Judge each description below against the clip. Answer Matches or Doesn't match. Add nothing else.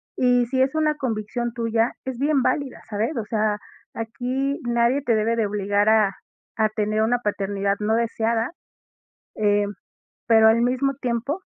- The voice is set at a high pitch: Matches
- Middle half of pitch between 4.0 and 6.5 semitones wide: Doesn't match